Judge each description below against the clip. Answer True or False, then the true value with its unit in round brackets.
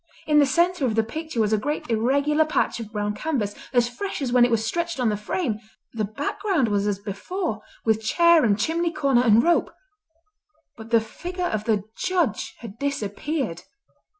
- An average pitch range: False (6.6 semitones)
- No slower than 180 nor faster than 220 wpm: True (185 wpm)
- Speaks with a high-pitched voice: True (245 Hz)